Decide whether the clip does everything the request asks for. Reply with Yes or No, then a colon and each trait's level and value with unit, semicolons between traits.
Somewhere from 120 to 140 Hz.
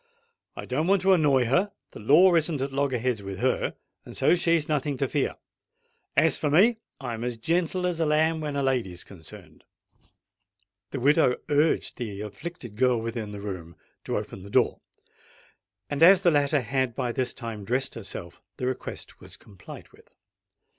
Yes: low, 135 Hz